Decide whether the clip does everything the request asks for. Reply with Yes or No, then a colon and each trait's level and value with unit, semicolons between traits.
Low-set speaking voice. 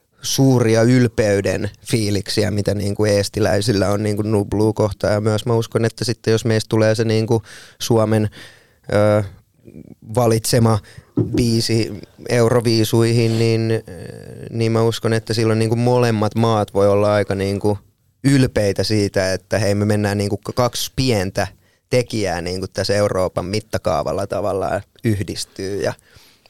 Yes: low, 110 Hz